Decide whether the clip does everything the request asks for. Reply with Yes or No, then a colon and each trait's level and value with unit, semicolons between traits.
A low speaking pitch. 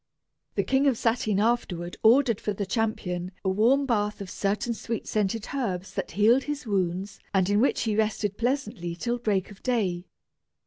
No: high, 215 Hz